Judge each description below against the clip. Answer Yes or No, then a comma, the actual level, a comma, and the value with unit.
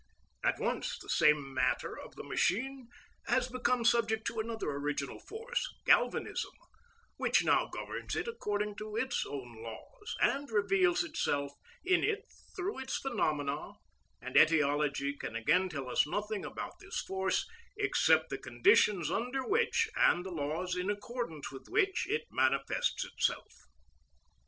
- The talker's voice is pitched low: No, high, 210 Hz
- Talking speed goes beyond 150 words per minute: No, average, 140 wpm